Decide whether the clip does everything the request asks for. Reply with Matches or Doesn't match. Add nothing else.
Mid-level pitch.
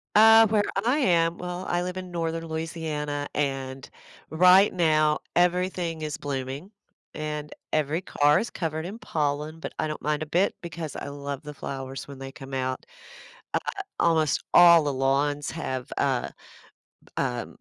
Matches